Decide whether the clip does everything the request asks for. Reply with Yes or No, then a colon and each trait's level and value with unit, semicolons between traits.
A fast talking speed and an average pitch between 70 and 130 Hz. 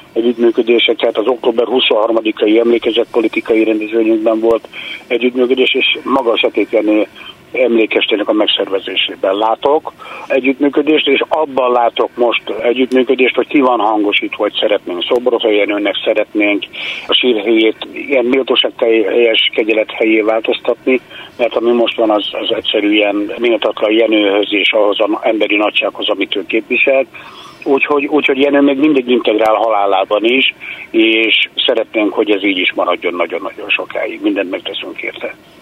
No: average, 130 wpm; low, 115 Hz